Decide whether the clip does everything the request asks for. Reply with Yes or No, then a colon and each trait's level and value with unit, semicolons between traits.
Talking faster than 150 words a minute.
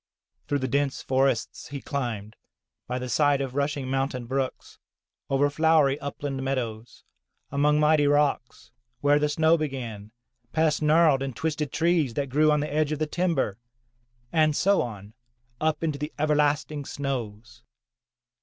No: average, 145 wpm